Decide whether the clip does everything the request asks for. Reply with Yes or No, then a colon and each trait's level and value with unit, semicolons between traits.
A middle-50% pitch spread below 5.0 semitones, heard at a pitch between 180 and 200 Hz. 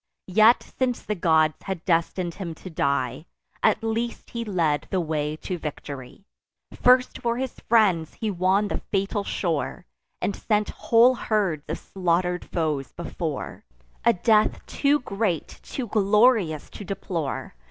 No: wide, 5.4 semitones; high, 190 Hz